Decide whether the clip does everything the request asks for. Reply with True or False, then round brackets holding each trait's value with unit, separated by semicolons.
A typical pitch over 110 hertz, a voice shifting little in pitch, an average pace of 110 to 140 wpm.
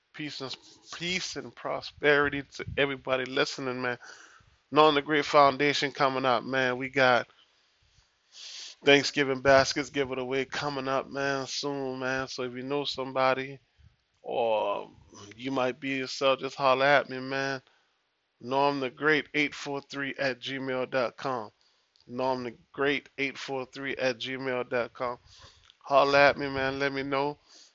True (135 Hz; 1.5 semitones; 135 wpm)